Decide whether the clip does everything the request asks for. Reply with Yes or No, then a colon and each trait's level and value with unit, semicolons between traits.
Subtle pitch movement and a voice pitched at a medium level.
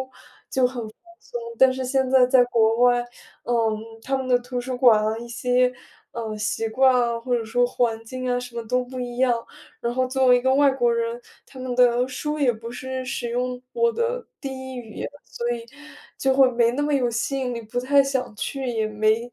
No: narrow, 1.9 semitones; high, 245 Hz